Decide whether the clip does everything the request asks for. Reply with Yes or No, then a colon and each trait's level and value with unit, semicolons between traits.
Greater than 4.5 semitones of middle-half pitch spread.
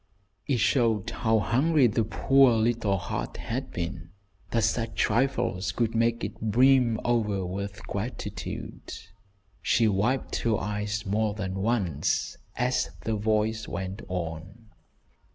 No: average, 2.9 semitones